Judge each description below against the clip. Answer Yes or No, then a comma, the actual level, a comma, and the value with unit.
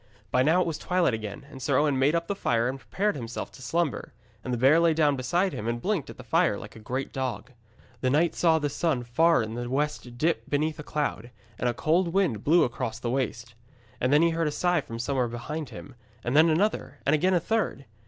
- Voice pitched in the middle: Yes, medium, 145 Hz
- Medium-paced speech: No, fast, 240 wpm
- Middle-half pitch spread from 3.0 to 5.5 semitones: Yes, average, 5.2 semitones